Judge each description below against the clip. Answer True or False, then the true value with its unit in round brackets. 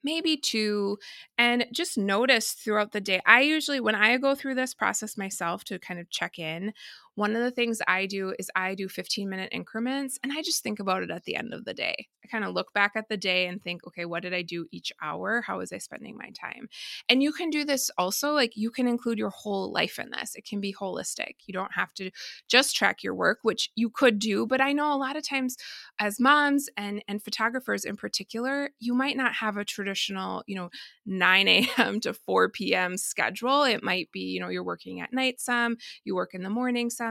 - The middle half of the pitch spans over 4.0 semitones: True (5.1 semitones)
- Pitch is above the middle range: True (220 Hz)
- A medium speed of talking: False (235 wpm)